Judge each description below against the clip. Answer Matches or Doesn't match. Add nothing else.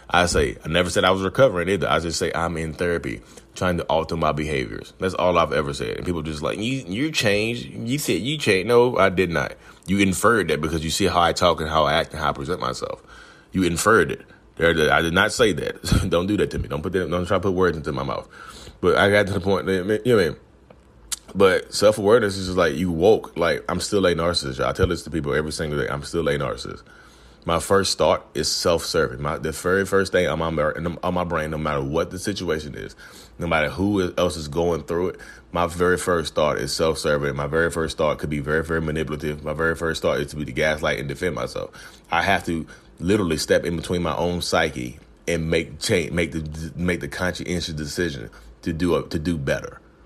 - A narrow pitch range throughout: Doesn't match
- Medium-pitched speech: Doesn't match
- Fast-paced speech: Matches